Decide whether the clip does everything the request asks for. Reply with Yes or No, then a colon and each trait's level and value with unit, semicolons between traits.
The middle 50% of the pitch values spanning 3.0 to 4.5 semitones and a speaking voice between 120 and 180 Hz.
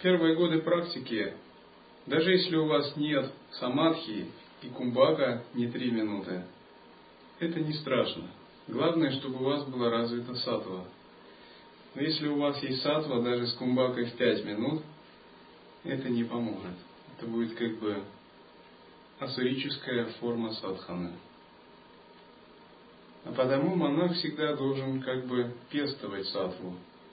No: average, 5.3 semitones; low, 125 Hz